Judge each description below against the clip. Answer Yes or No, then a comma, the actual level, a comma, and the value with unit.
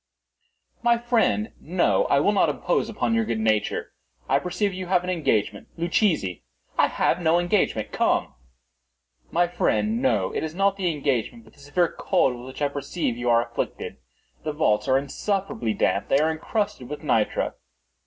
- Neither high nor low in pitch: Yes, medium, 165 Hz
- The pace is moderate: Yes, average, 170 wpm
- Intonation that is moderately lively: No, wide, 7.1 semitones